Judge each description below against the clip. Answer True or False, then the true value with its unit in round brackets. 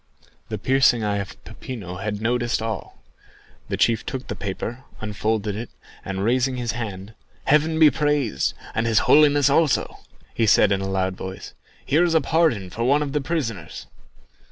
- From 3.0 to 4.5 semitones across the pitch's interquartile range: False (5.5 semitones)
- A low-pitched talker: True (115 Hz)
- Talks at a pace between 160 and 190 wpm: True (170 wpm)